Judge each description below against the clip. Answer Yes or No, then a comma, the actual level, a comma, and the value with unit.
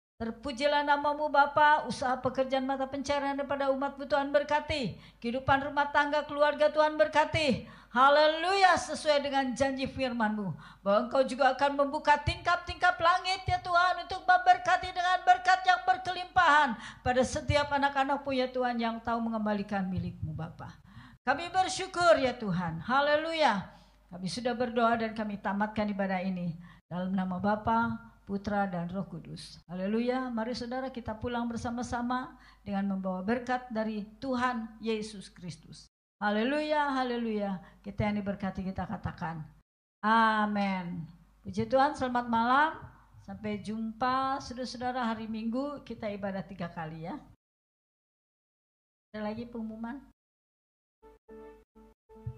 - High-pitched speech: Yes, high, 245 Hz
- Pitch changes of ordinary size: No, wide, 5.7 semitones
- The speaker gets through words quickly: No, average, 120 wpm